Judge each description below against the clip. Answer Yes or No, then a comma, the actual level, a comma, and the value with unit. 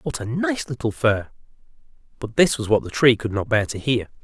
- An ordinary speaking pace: No, fast, 225 wpm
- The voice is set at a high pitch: No, low, 115 Hz